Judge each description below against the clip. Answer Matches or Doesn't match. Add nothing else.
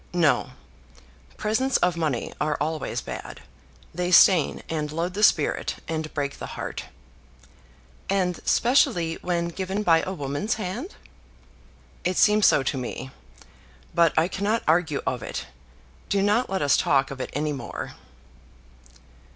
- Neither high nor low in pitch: Matches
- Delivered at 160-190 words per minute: Doesn't match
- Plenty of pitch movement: Doesn't match